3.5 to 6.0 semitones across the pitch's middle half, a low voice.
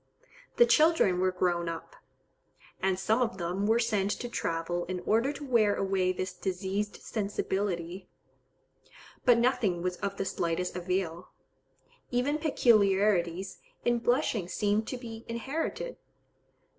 No: average, 4.4 semitones; high, 195 Hz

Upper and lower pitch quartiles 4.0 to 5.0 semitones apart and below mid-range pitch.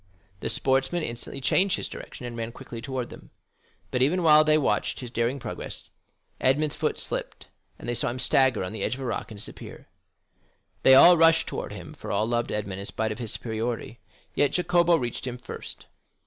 Yes: average, 4.5 semitones; low, 130 Hz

